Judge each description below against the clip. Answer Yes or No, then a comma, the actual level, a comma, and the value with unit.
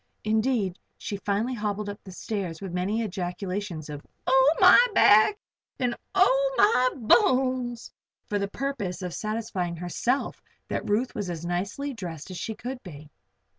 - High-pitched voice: Yes, high, 210 Hz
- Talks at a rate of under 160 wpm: Yes, average, 145 wpm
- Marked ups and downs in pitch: Yes, wide, 5.7 semitones